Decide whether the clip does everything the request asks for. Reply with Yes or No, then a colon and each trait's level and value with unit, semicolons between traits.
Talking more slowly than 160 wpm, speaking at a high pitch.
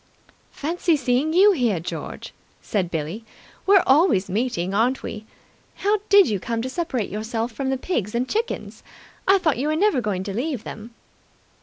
No: average, 170 wpm; very high, 250 Hz